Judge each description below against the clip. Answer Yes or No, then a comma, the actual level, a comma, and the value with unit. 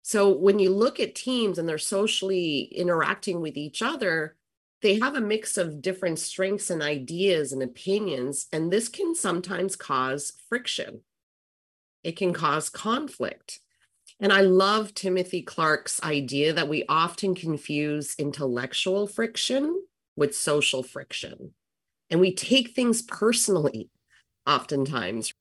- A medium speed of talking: No, slow, 130 wpm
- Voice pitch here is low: No, medium, 180 Hz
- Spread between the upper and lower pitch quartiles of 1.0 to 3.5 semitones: No, wide, 5.4 semitones